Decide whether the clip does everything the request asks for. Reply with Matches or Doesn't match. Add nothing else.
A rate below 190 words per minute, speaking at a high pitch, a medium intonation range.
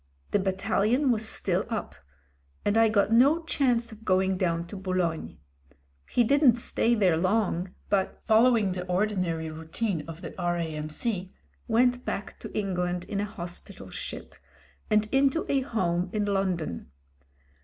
Matches